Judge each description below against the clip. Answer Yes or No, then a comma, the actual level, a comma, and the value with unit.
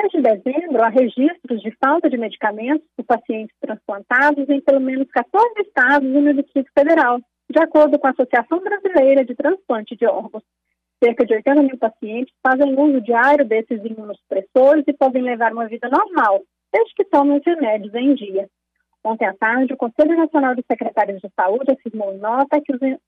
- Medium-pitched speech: No, very high, 265 Hz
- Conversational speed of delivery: Yes, average, 170 wpm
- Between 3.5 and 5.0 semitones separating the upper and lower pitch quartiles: Yes, average, 4.3 semitones